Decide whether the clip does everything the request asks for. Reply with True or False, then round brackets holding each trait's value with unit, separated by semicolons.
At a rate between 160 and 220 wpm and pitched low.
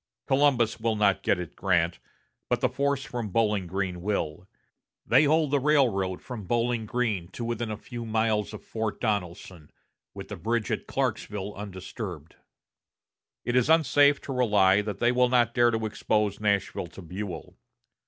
True (165 wpm; 110 Hz)